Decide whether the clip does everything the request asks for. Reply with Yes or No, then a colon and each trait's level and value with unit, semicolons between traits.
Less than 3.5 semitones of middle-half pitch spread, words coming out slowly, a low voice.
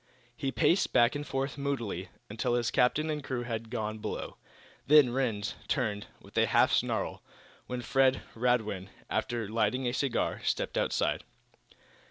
No: average, 3.0 semitones; average, 150 wpm; low, 125 Hz